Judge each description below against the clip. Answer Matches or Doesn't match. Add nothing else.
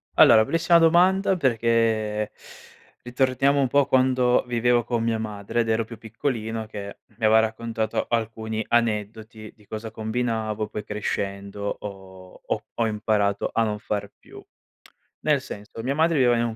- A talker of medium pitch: Doesn't match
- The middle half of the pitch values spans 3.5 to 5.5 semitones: Doesn't match